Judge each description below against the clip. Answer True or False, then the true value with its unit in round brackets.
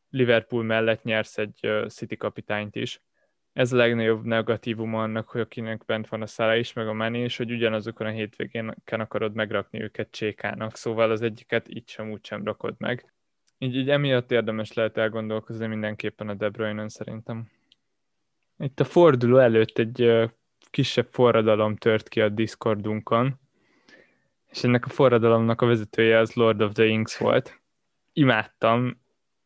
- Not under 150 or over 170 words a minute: True (155 wpm)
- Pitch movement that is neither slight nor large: False (1.5 semitones)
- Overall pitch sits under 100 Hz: False (115 Hz)